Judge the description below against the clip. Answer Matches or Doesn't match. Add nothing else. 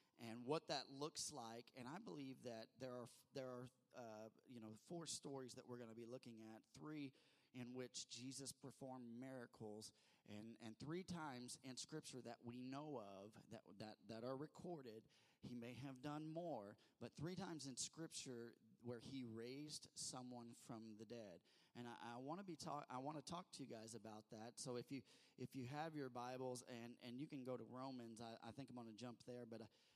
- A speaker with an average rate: Doesn't match